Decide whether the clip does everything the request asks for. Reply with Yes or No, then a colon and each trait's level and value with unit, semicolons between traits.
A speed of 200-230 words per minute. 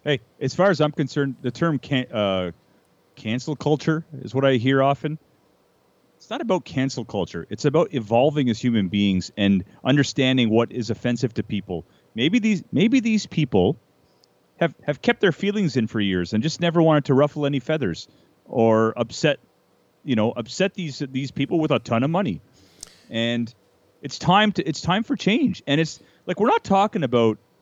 No: average, 185 wpm